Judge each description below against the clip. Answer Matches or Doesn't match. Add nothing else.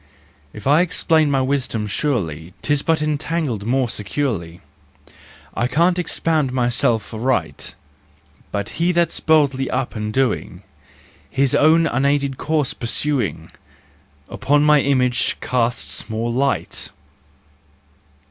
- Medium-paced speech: Doesn't match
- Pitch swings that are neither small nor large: Matches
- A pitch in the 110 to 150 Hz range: Matches